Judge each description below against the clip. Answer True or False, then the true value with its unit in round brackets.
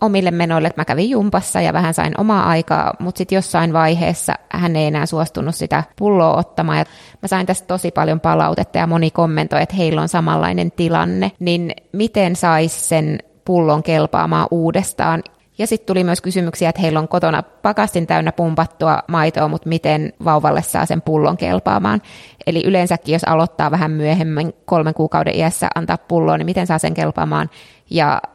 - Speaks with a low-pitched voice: False (165 Hz)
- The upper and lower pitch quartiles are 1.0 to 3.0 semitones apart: True (2.6 semitones)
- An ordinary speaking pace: False (170 wpm)